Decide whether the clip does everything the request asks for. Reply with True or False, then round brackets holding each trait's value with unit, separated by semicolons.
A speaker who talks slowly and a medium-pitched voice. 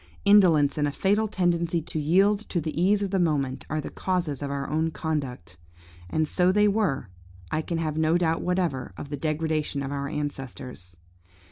False (190 wpm; 160 Hz)